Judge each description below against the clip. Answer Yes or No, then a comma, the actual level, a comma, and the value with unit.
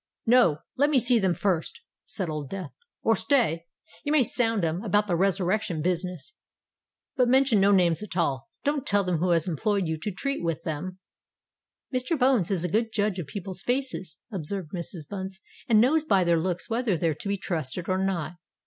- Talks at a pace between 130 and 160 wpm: No, average, 185 wpm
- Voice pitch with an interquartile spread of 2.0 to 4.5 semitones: No, average, 5.1 semitones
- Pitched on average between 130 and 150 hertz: No, high, 190 Hz